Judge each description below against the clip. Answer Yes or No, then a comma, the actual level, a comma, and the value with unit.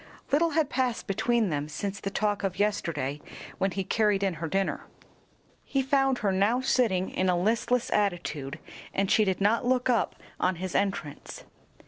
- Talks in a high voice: Yes, high, 200 Hz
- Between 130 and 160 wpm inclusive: No, average, 170 wpm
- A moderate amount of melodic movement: Yes, average, 4.5 semitones